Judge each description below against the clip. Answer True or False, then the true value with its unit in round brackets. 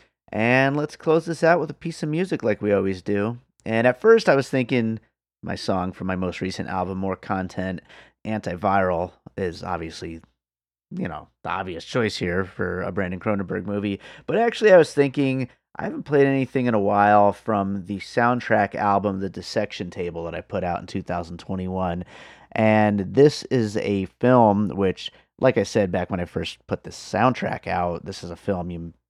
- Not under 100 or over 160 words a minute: False (185 wpm)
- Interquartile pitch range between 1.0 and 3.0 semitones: False (5.1 semitones)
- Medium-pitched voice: False (100 Hz)